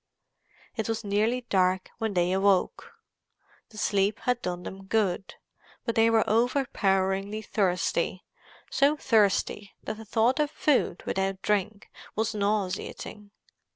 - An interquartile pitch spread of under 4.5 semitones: Yes, average, 2.7 semitones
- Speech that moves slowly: Yes, slow, 120 wpm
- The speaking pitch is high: Yes, high, 210 Hz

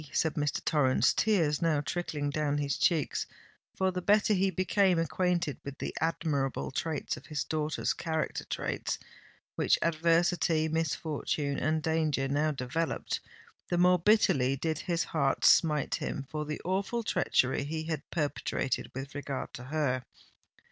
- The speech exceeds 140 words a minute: No, slow, 135 wpm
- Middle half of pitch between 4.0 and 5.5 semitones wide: No, average, 3.0 semitones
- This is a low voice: No, medium, 155 Hz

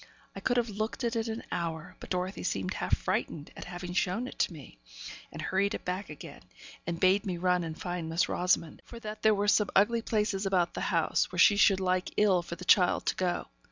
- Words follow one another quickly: Yes, fast, 230 wpm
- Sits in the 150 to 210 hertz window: Yes, medium, 185 Hz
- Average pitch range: Yes, average, 3.0 semitones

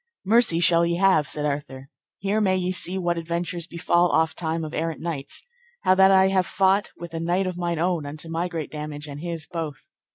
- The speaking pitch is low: No, medium, 170 Hz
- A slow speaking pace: No, fast, 205 wpm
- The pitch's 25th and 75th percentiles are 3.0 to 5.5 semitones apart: No, narrow, 2.6 semitones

